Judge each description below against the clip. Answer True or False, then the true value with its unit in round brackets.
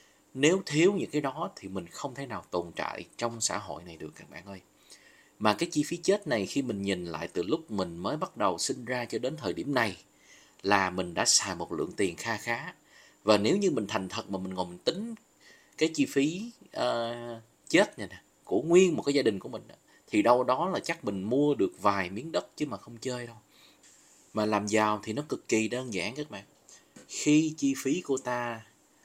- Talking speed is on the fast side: False (225 wpm)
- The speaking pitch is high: False (120 Hz)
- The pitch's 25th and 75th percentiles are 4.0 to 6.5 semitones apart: False (6.9 semitones)